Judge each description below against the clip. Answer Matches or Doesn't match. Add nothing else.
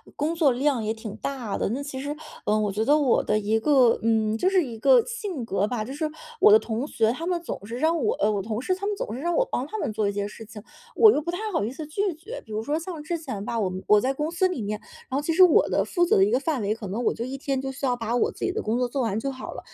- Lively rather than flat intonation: Matches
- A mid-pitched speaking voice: Doesn't match